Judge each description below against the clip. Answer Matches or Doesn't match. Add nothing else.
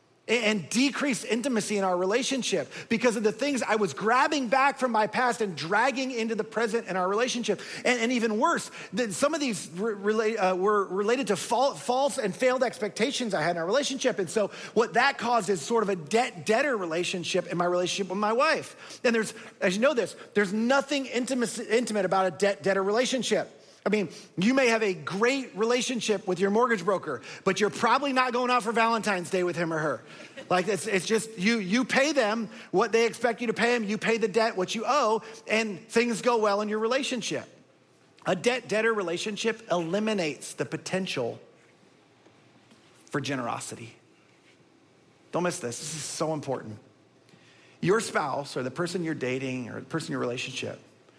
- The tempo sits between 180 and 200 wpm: Matches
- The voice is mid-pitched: Doesn't match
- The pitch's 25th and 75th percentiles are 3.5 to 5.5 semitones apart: Matches